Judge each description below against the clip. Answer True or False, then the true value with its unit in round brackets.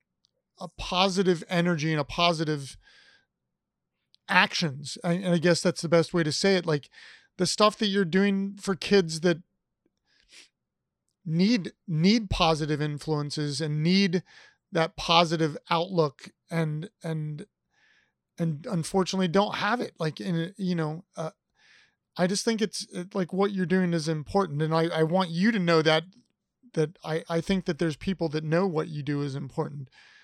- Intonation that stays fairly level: False (3.4 semitones)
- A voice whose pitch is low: False (170 Hz)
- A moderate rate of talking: True (160 wpm)